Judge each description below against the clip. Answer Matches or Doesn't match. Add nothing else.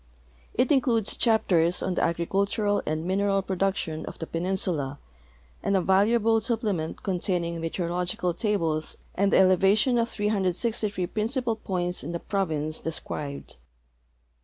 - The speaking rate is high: Doesn't match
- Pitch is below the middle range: Doesn't match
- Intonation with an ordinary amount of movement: Matches